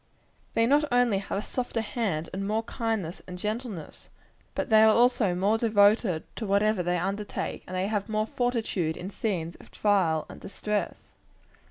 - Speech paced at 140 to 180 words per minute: Yes, average, 170 wpm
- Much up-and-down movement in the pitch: No, average, 3.4 semitones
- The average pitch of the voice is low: No, high, 210 Hz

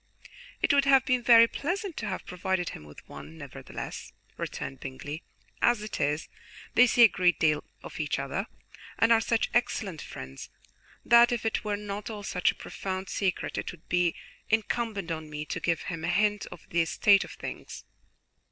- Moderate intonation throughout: No, wide, 6.1 semitones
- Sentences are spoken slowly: No, average, 185 wpm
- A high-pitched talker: Yes, high, 195 Hz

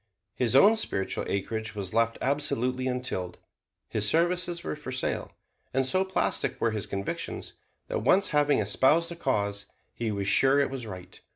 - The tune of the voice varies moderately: No, wide, 5.9 semitones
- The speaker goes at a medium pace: Yes, average, 165 wpm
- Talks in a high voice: No, low, 125 Hz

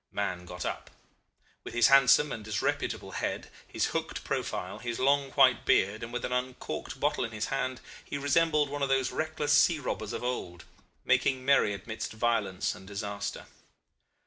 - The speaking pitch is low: Yes, low, 125 Hz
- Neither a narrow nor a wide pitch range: Yes, average, 4.6 semitones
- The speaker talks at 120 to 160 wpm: No, average, 170 wpm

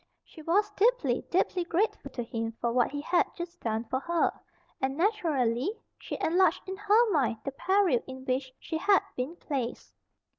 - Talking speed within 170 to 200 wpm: Yes, average, 175 wpm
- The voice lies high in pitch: Yes, very high, 320 Hz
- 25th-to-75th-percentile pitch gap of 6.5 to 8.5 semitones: Yes, wide, 7.0 semitones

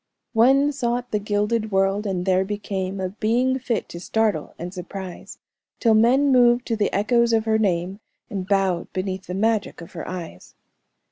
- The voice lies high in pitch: Yes, high, 205 Hz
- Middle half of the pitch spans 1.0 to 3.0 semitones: No, average, 3.7 semitones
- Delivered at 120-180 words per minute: Yes, average, 175 wpm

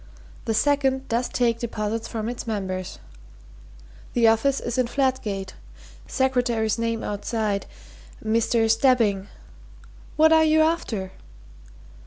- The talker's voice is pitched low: No, high, 230 Hz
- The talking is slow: Yes, slow, 110 wpm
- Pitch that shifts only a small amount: No, average, 3.3 semitones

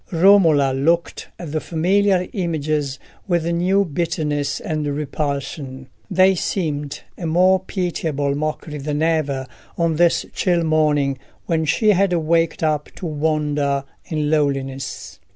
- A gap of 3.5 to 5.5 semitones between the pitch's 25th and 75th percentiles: No, average, 2.9 semitones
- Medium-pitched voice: Yes, medium, 155 Hz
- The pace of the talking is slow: Yes, slow, 125 wpm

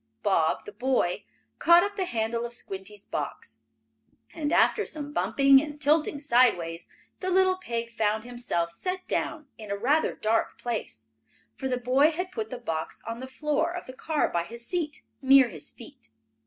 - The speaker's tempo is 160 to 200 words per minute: Yes, average, 175 wpm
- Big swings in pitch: Yes, wide, 5.9 semitones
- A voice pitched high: Yes, very high, 250 Hz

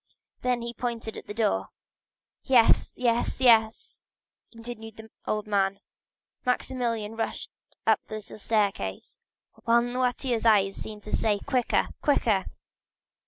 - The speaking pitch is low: No, high, 225 Hz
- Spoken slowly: Yes, slow, 120 wpm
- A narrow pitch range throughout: Yes, narrow, 2.3 semitones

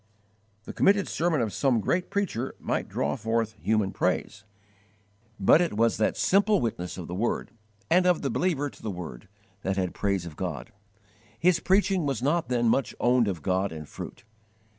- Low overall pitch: Yes, low, 120 Hz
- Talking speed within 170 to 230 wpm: Yes, average, 180 wpm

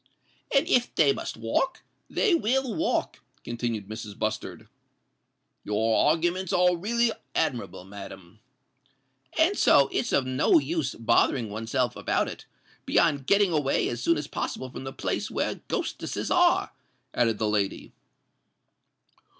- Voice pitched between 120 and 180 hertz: Yes, low, 135 Hz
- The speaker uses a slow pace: Yes, slow, 130 wpm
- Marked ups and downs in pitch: Yes, wide, 9.0 semitones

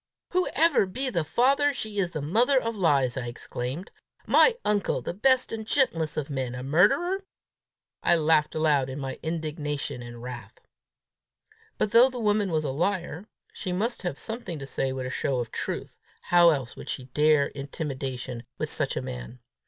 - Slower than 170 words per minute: No, average, 175 wpm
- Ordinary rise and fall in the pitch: No, wide, 7.9 semitones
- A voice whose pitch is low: No, medium, 160 Hz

